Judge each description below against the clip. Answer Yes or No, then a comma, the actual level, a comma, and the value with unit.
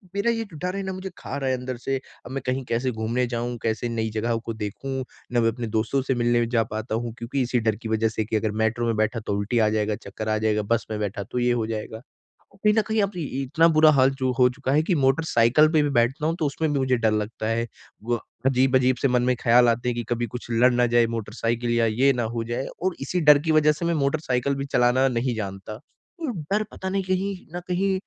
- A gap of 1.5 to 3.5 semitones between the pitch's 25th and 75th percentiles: No, average, 3.9 semitones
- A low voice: Yes, low, 125 Hz